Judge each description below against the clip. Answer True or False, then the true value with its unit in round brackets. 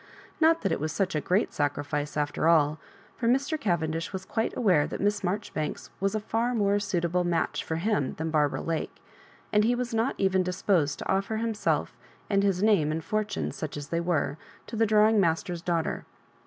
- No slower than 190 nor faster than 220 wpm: True (200 wpm)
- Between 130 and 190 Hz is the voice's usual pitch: True (185 Hz)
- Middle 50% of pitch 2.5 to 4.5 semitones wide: False (5.0 semitones)